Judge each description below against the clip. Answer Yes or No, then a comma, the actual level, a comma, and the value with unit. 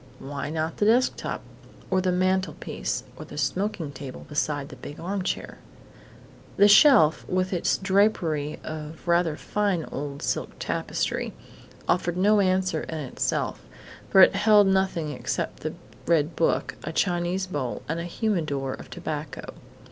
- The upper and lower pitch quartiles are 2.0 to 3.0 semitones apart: No, average, 4.0 semitones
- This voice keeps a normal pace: Yes, average, 145 wpm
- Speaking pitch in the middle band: Yes, medium, 175 Hz